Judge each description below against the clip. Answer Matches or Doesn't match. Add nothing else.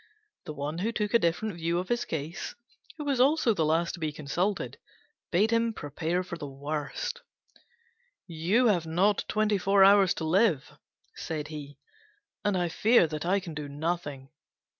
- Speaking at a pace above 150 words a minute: Matches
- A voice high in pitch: Doesn't match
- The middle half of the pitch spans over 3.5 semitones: Matches